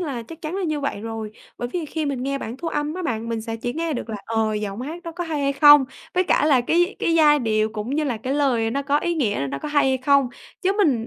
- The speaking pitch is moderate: No, very high, 275 Hz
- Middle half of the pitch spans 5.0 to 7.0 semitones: Yes, wide, 5.4 semitones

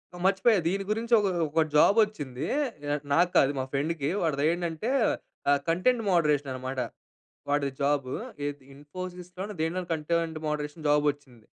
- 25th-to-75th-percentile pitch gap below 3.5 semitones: No, average, 4.0 semitones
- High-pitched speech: No, medium, 160 Hz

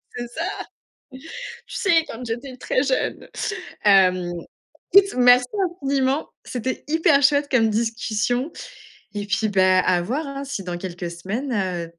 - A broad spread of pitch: Yes, wide, 6.2 semitones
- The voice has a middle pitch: No, high, 245 Hz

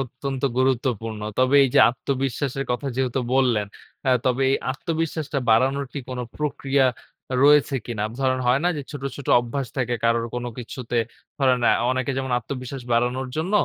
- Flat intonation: Yes, narrow, 2.0 semitones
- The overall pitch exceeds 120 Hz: Yes, low, 130 Hz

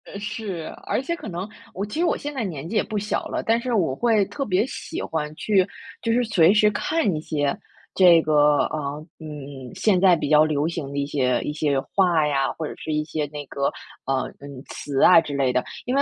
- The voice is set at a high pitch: No, medium, 160 Hz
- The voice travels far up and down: Yes, wide, 6.3 semitones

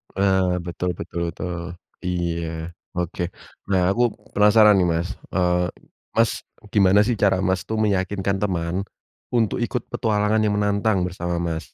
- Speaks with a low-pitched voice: Yes, very low, 95 Hz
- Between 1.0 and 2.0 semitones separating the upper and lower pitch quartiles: No, average, 2.7 semitones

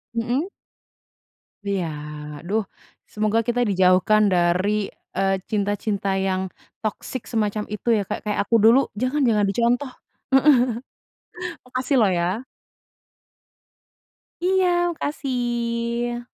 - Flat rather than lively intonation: No, average, 3.6 semitones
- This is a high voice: Yes, high, 220 Hz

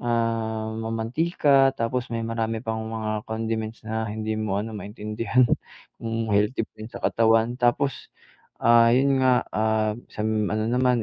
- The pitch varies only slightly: Yes, narrow, 1.4 semitones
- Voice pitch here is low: Yes, low, 115 Hz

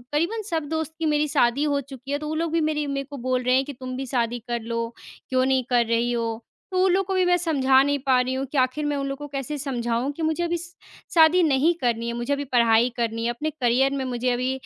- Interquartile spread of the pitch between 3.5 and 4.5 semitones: Yes, average, 3.8 semitones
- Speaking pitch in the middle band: No, very high, 270 Hz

